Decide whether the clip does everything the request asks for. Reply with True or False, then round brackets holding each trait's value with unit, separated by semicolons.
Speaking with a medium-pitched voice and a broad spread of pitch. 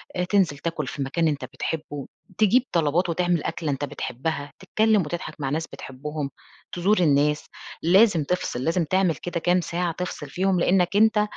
False (170 Hz; 3.7 semitones)